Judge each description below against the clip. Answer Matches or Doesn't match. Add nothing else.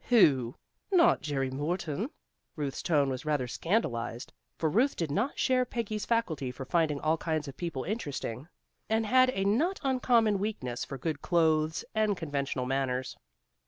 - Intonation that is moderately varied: Doesn't match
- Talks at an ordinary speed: Matches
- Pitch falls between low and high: Matches